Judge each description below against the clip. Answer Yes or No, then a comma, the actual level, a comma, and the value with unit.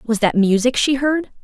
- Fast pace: Yes, fast, 210 wpm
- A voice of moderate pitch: No, high, 240 Hz